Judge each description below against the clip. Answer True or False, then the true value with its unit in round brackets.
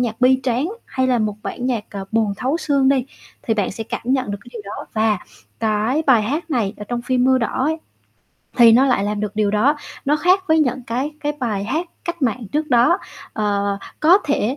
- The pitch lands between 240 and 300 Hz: True (245 Hz)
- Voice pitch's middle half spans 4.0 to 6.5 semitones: True (4.4 semitones)